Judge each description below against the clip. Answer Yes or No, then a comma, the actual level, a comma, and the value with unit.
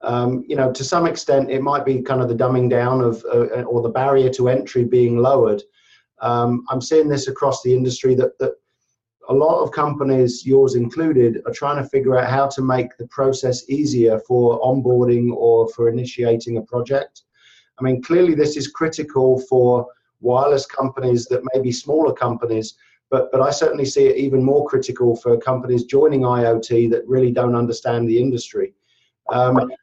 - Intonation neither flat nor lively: No, narrow, 2.2 semitones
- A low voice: Yes, low, 130 Hz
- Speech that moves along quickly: No, average, 180 wpm